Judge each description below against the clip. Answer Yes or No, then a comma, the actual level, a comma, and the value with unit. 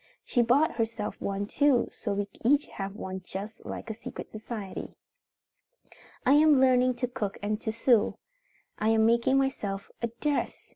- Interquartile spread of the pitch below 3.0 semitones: No, average, 3.8 semitones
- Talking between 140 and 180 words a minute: Yes, average, 160 wpm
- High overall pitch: Yes, high, 230 Hz